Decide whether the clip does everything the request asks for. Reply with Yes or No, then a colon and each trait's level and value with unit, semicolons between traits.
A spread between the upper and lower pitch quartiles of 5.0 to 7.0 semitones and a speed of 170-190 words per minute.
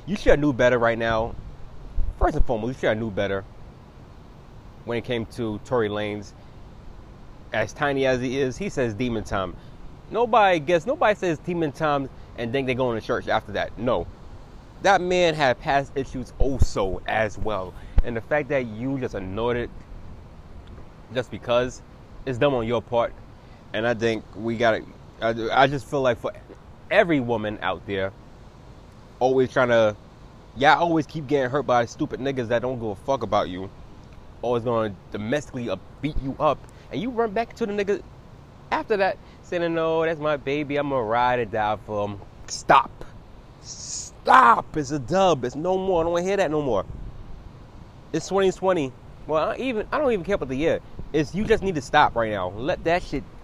Yes: average, 5.3 semitones; average, 185 wpm